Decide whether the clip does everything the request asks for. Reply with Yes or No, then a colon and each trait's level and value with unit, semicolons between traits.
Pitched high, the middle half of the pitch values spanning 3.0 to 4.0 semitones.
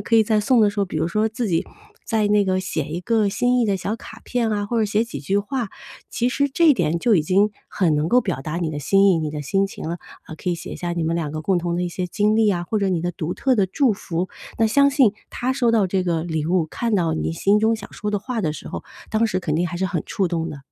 No: high, 195 Hz; average, 4.6 semitones